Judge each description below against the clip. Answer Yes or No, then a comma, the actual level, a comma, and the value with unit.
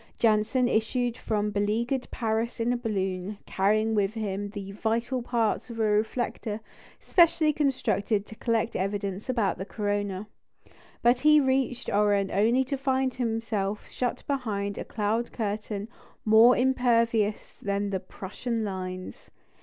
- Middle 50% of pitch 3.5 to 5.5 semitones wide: No, average, 3.1 semitones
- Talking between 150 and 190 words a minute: No, slow, 135 wpm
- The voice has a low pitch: No, high, 220 Hz